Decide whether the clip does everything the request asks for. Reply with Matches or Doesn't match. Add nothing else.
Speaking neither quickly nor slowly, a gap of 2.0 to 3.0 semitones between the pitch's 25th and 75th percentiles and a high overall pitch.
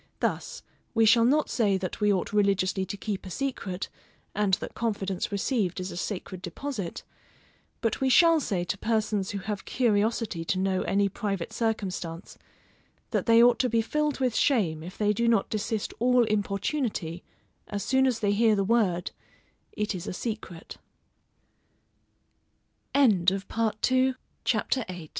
Doesn't match